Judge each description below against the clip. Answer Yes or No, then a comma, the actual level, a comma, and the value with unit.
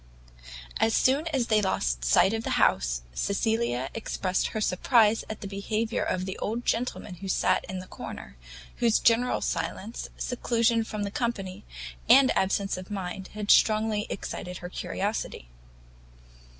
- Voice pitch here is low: No, high, 210 Hz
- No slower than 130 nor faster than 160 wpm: Yes, average, 150 wpm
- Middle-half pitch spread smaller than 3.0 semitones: No, average, 3.5 semitones